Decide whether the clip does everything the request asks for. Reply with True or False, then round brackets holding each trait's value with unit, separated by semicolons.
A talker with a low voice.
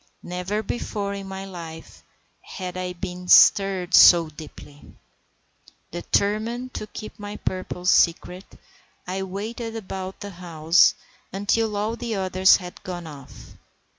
False (190 Hz)